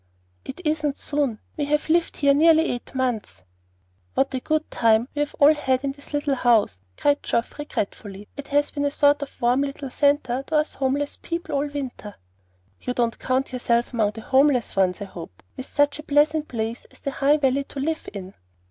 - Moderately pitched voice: No, very high, 275 Hz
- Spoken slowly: No, average, 200 wpm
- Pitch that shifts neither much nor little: Yes, average, 3.3 semitones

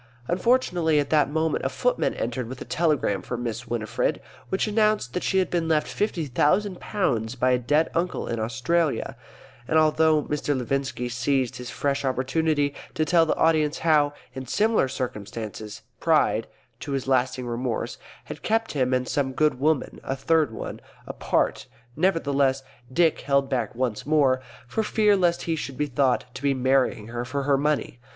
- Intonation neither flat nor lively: Yes, average, 4.1 semitones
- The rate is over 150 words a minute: Yes, average, 175 wpm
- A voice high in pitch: No, medium, 140 Hz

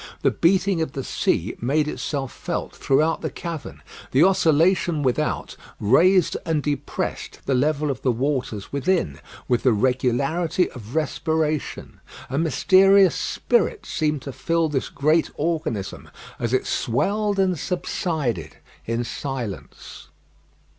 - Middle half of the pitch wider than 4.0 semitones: Yes, average, 4.7 semitones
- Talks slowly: Yes, slow, 125 wpm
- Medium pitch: Yes, medium, 150 Hz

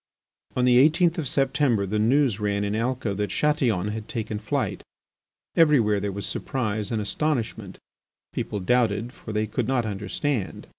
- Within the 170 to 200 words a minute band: No, average, 155 wpm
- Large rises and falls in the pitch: No, average, 4.2 semitones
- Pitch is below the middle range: Yes, low, 110 Hz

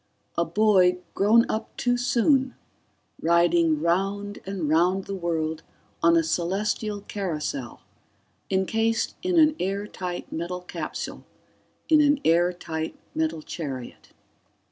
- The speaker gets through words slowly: Yes, slow, 110 wpm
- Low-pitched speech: No, medium, 180 Hz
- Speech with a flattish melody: No, average, 4.1 semitones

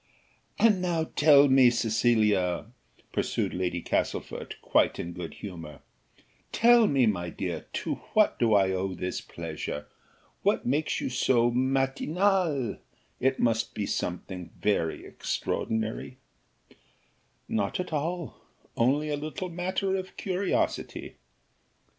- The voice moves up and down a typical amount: No, wide, 8.4 semitones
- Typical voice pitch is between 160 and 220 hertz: No, low, 125 Hz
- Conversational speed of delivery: No, slow, 115 wpm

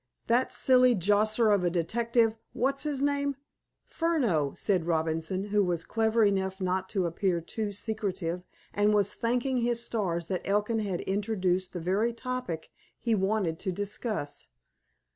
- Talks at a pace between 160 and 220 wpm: No, average, 145 wpm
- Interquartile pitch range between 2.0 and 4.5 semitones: Yes, average, 4.2 semitones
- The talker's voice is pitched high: Yes, high, 205 Hz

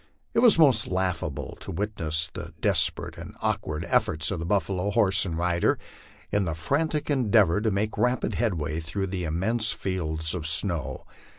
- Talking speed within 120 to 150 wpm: No, average, 165 wpm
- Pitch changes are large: No, average, 4.6 semitones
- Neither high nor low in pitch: No, very low, 95 Hz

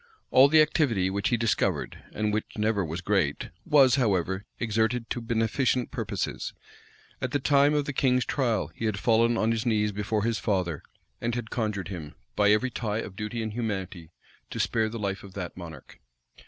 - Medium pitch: No, low, 110 Hz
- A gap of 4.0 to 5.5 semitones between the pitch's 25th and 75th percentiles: No, average, 3.3 semitones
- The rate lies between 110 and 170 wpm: No, average, 185 wpm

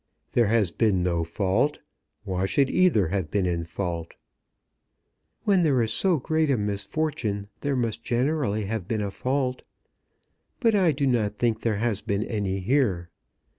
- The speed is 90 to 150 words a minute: No, average, 160 wpm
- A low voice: Yes, low, 110 Hz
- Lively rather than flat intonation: Yes, wide, 5.9 semitones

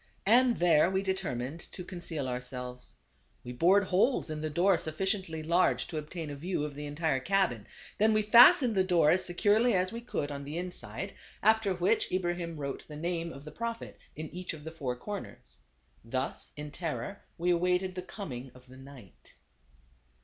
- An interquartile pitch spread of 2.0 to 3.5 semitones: No, average, 4.6 semitones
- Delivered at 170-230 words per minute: Yes, average, 185 wpm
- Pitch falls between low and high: Yes, medium, 170 Hz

